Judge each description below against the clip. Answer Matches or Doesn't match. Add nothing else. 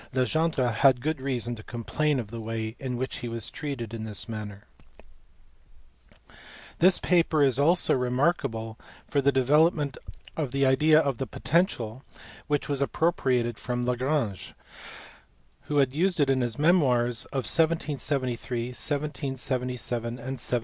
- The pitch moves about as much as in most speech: Matches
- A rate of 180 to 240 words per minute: Doesn't match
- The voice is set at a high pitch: Doesn't match